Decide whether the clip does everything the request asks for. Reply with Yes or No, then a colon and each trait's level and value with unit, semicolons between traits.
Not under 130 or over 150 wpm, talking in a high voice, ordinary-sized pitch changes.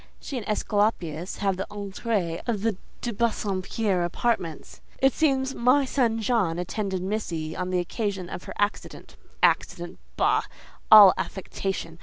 Yes: slow, 135 wpm; high, 200 Hz; average, 4.0 semitones